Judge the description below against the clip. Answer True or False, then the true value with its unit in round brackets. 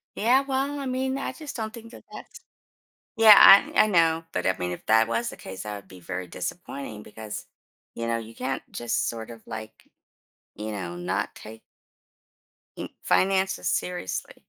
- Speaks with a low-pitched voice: True (115 Hz)